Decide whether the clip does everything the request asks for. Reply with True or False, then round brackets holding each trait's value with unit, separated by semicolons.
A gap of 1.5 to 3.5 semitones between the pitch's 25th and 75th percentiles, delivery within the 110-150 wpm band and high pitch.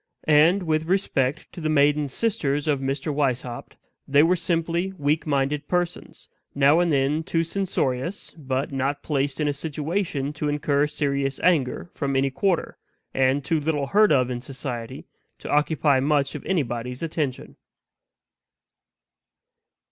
False (2.9 semitones; 140 wpm; 145 Hz)